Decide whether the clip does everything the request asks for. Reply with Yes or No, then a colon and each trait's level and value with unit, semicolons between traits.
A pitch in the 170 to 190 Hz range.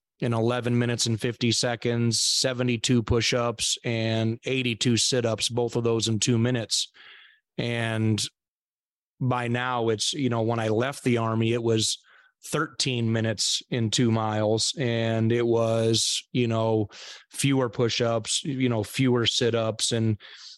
No: low, 115 Hz